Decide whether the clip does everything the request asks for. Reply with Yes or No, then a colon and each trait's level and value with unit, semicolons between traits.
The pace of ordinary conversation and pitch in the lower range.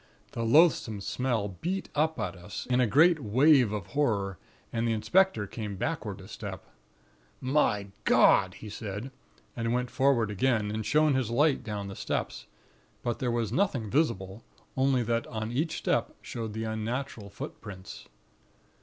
Yes: average, 155 wpm; low, 115 Hz